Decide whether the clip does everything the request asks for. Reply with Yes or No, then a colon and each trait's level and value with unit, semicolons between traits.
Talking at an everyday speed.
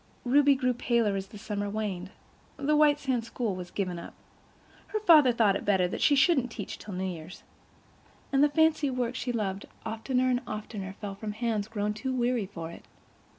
Yes: average, 185 wpm